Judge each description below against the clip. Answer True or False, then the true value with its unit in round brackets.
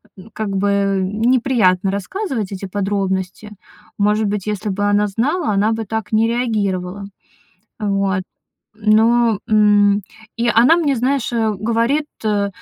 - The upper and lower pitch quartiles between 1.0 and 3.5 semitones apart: True (2.5 semitones)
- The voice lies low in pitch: False (210 Hz)